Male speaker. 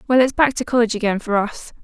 No: female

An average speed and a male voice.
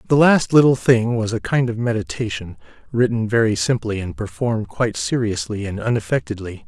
Yes: average, 160 wpm; male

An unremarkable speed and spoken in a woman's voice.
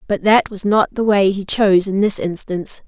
No: fast, 230 wpm; female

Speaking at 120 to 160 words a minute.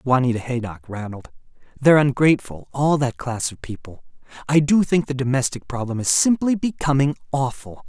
Yes: average, 150 wpm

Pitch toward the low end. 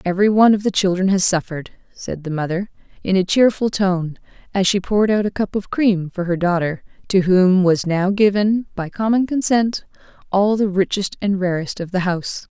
No: high, 190 Hz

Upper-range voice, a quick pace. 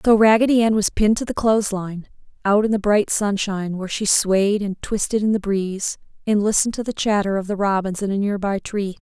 Yes: high, 205 Hz; fast, 225 wpm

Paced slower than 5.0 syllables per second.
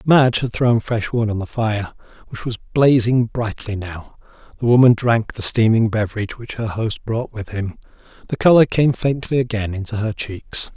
Yes: 4.8 syllables/s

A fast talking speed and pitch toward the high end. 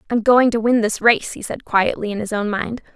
Yes: fast, 265 wpm; high, 225 Hz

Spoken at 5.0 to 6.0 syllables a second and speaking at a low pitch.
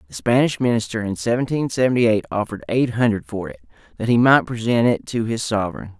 No: 6.2 syllables/s; low, 115 Hz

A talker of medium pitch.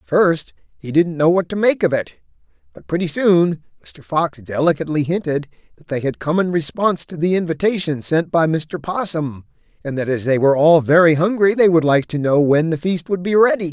Yes: medium, 160 Hz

